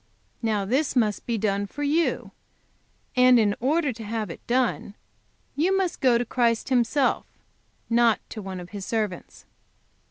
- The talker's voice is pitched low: No, high, 235 Hz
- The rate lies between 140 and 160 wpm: Yes, average, 155 wpm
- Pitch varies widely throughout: No, average, 3.8 semitones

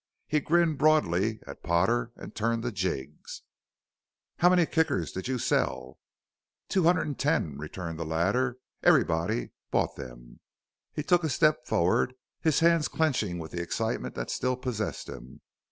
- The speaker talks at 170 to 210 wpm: No, average, 155 wpm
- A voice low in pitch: Yes, low, 115 Hz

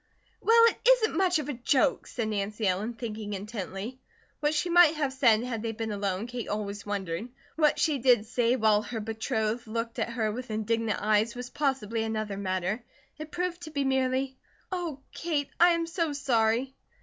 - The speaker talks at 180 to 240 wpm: Yes, average, 185 wpm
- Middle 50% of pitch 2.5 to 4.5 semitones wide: No, average, 5.1 semitones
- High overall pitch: Yes, high, 235 Hz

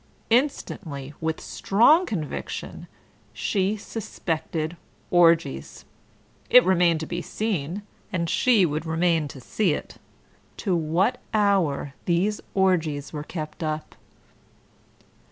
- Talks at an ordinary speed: No, slow, 105 wpm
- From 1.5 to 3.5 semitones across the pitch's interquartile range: No, average, 4.3 semitones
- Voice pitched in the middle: Yes, medium, 170 Hz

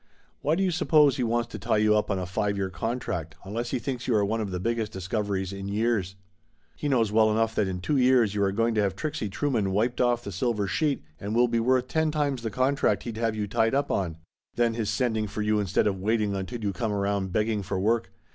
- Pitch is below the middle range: Yes, low, 110 Hz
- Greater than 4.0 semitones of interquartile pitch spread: No, average, 3.3 semitones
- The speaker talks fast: Yes, fast, 255 wpm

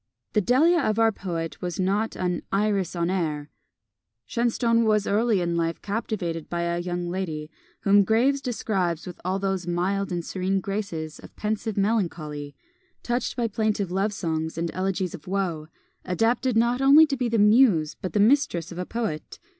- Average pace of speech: Yes, average, 170 wpm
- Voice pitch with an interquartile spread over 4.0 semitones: Yes, average, 4.4 semitones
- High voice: Yes, high, 195 Hz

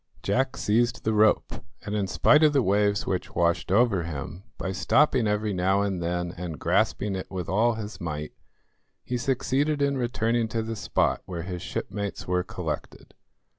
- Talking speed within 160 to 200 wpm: Yes, average, 170 wpm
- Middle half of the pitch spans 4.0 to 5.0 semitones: Yes, average, 4.6 semitones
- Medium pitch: No, low, 105 Hz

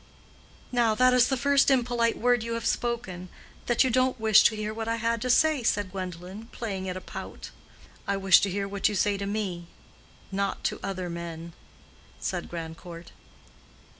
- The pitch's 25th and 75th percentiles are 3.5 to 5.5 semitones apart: Yes, average, 4.2 semitones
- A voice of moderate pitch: No, high, 215 Hz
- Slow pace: No, average, 170 wpm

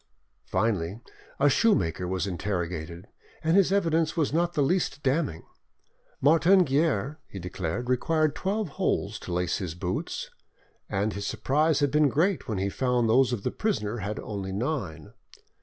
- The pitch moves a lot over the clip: Yes, wide, 8.8 semitones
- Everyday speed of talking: Yes, average, 155 wpm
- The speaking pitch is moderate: No, low, 125 Hz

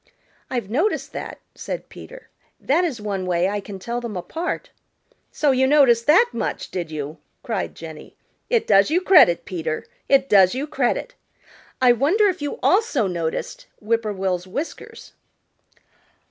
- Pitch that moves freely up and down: Yes, wide, 8.4 semitones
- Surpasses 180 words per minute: No, average, 155 wpm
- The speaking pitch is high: Yes, high, 235 Hz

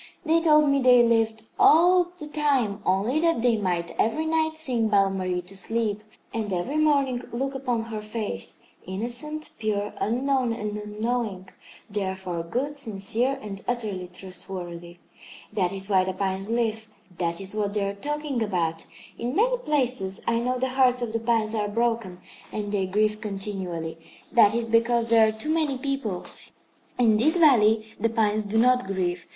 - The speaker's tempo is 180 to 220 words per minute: No, average, 170 wpm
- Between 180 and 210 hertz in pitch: No, high, 220 Hz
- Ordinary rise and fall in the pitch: Yes, average, 4.4 semitones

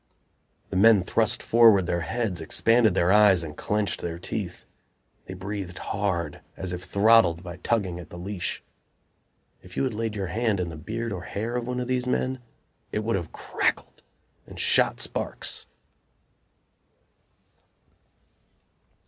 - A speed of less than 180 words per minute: Yes, average, 150 wpm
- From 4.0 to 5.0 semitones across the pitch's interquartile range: Yes, average, 4.3 semitones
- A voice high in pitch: No, low, 100 Hz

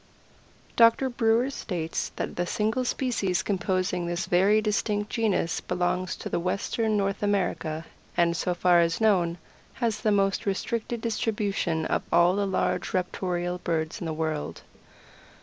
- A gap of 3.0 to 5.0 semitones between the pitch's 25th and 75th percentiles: Yes, average, 3.6 semitones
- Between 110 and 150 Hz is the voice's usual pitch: No, high, 190 Hz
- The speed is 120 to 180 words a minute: Yes, average, 140 wpm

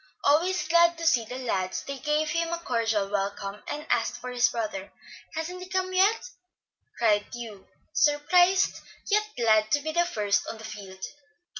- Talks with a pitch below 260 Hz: No, very high, 275 Hz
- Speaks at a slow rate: No, average, 170 wpm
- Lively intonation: Yes, wide, 8.0 semitones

